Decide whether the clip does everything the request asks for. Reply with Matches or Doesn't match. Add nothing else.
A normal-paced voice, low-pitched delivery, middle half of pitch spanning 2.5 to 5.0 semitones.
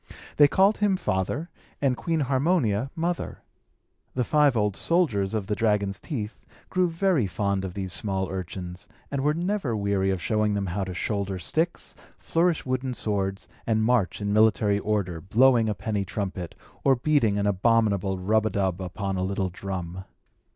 Doesn't match